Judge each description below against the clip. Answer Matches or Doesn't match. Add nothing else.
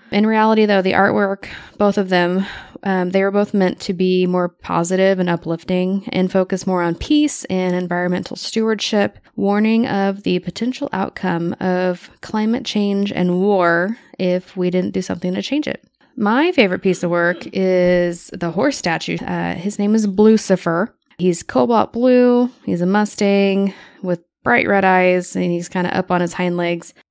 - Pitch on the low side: Doesn't match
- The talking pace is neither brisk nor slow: Matches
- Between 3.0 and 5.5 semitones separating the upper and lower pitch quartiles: Doesn't match